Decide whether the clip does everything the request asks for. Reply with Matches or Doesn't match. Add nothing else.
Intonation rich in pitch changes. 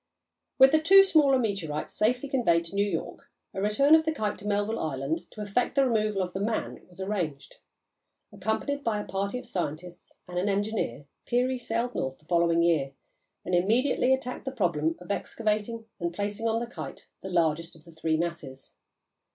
Matches